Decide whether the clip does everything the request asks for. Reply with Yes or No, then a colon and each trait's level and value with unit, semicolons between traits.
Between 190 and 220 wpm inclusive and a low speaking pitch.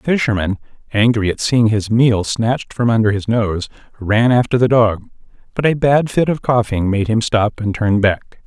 Yes: average, 200 wpm; low, 110 Hz